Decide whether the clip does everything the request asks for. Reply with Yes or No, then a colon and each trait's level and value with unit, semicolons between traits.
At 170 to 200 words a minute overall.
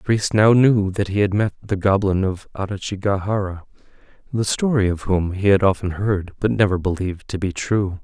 Yes: average, 195 wpm